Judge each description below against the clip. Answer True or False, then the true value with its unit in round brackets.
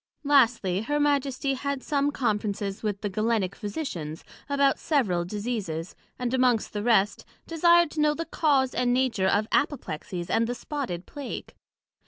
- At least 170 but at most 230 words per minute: False (150 wpm)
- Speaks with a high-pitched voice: True (245 Hz)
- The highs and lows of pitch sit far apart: True (5.7 semitones)